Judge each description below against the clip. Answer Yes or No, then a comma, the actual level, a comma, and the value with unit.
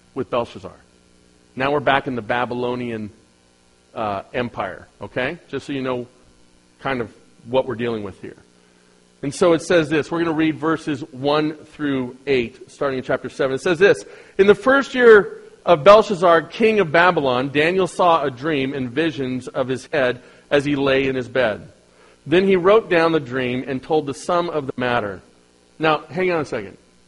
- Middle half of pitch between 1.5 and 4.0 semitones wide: No, wide, 5.6 semitones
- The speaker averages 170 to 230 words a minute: Yes, average, 185 wpm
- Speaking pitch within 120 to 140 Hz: Yes, low, 135 Hz